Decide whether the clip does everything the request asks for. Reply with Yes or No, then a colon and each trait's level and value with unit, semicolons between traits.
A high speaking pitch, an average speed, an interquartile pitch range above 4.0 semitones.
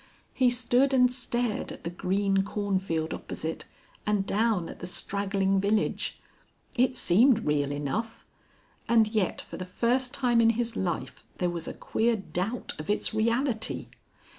Yes: high, 210 Hz; average, 150 wpm; average, 4.5 semitones